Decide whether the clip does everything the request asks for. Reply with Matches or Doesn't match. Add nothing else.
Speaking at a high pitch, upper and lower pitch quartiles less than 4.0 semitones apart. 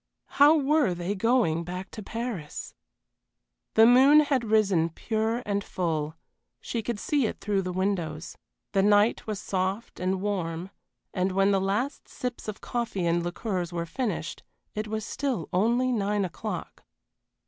Doesn't match